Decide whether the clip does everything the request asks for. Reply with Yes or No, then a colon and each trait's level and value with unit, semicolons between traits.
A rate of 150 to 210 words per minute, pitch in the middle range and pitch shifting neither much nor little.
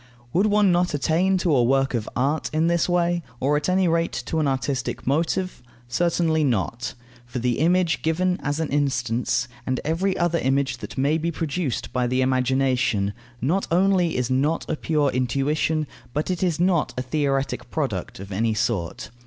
Yes: average, 175 wpm; medium, 145 Hz; average, 5.0 semitones